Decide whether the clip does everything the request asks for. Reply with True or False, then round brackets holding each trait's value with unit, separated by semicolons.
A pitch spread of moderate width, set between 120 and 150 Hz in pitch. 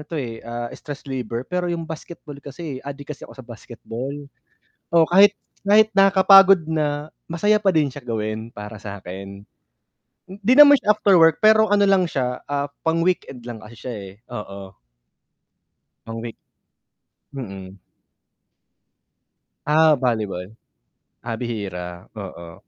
False (7.3 semitones; 140 Hz)